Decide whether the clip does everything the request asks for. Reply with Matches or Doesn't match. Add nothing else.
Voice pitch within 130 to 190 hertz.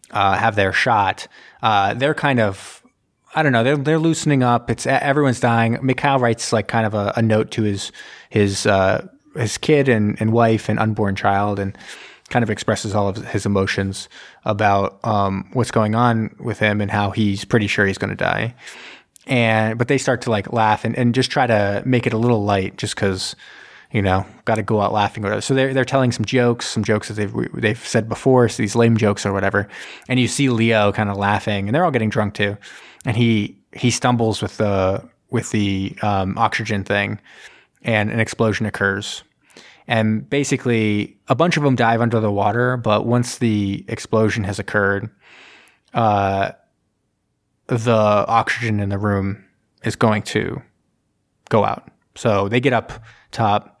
Doesn't match